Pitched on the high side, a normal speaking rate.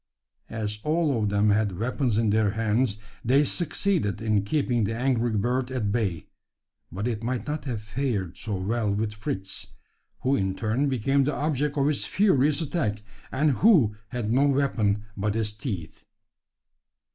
No: low, 115 Hz; average, 160 wpm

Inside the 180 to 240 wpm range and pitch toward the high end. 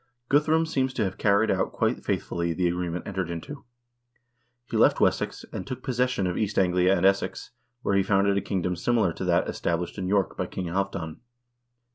No: average, 185 wpm; very low, 95 Hz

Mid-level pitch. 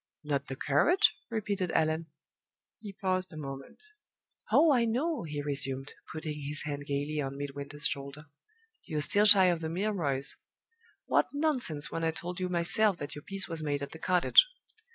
Yes: medium, 160 Hz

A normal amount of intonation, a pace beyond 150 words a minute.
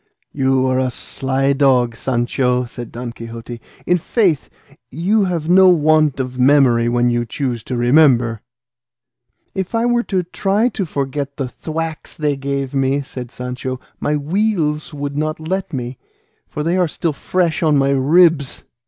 Yes: average, 4.4 semitones; average, 160 wpm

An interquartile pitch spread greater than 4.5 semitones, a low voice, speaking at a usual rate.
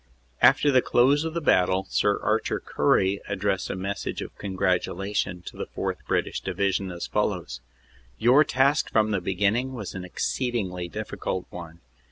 Yes: average, 4.9 semitones; low, 100 Hz; average, 160 wpm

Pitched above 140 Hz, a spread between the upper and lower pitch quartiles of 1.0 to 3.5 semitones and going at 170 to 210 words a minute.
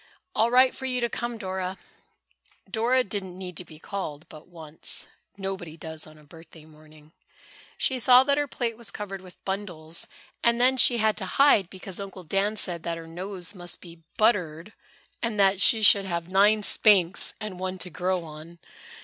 No: high, 190 Hz; average, 4.4 semitones; average, 185 wpm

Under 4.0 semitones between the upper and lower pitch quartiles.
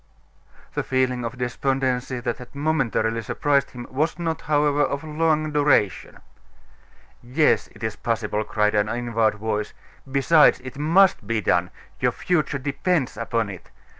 No: average, 4.6 semitones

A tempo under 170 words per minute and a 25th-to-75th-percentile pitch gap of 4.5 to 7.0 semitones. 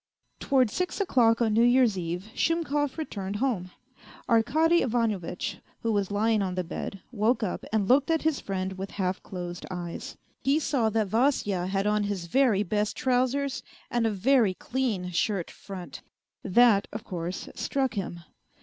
Yes: average, 160 wpm; average, 5.2 semitones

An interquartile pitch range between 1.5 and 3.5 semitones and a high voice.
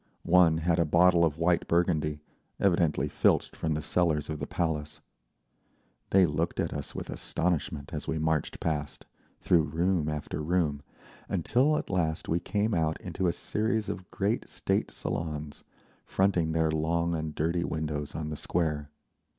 No: narrow, 2.4 semitones; very low, 80 Hz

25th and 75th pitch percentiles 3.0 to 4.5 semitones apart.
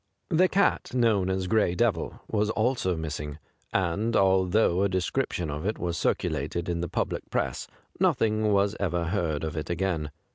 Yes: average, 4.1 semitones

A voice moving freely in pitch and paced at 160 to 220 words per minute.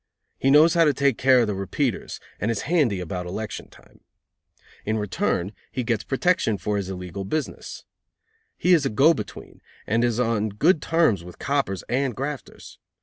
Yes: wide, 5.8 semitones; average, 175 wpm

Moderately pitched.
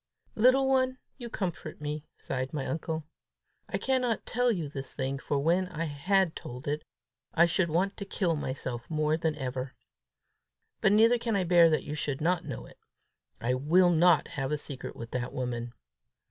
Yes: medium, 160 Hz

